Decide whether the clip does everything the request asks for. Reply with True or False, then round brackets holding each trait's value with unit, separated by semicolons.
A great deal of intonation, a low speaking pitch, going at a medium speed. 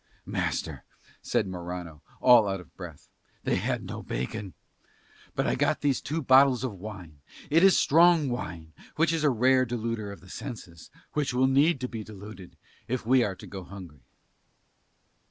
True (6.3 semitones; 115 Hz; 170 wpm)